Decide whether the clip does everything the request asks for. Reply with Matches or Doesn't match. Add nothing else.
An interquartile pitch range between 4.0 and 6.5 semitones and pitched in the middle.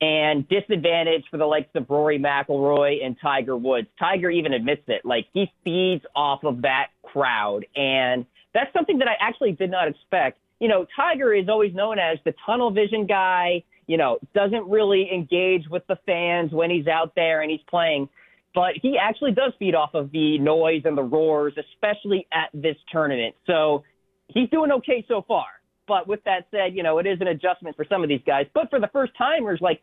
Matches